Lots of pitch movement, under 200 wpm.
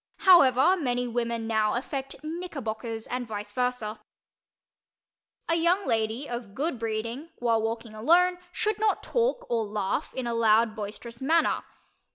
Yes: wide, 6.0 semitones; average, 140 wpm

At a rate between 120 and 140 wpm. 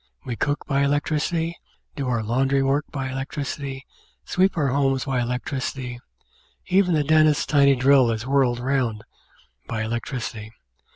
Yes: slow, 135 wpm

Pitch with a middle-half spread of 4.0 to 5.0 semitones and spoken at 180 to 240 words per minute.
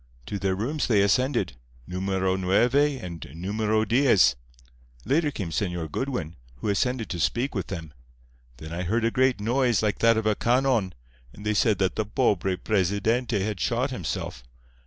No: average, 4.7 semitones; average, 160 wpm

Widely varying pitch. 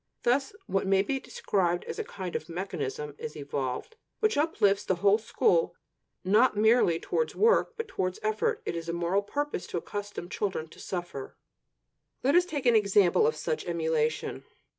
Yes: wide, 7.3 semitones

